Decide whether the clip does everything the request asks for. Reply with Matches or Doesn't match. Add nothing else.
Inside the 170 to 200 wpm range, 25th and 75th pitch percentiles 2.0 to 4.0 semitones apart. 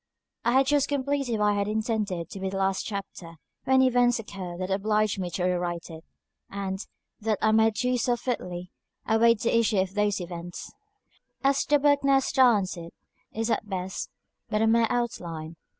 Doesn't match